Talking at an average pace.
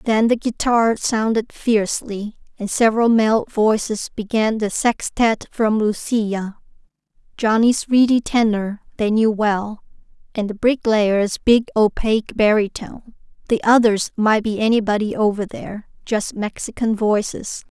No: slow, 120 wpm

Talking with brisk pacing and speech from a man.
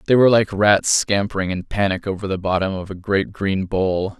Yes: fast, 215 wpm; male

